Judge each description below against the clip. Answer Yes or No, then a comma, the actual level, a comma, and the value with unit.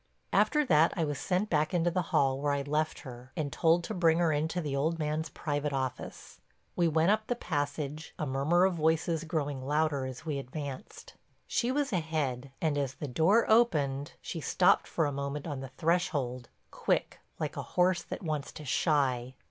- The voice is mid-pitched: Yes, medium, 150 Hz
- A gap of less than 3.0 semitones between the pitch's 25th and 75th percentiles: No, average, 3.3 semitones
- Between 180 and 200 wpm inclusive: Yes, average, 190 wpm